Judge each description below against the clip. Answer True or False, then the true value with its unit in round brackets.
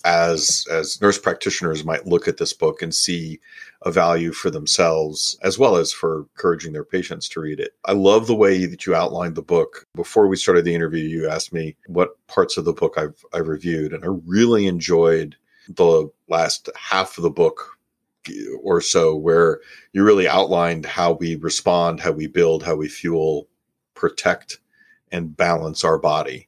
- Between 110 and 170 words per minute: False (180 wpm)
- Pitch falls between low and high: False (90 Hz)